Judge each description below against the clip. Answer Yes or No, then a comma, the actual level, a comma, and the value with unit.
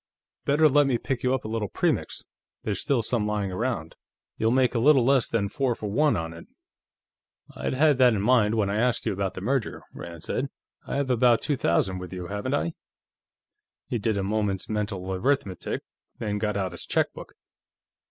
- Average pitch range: Yes, average, 4.6 semitones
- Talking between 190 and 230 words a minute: Yes, average, 195 wpm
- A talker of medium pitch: No, low, 110 Hz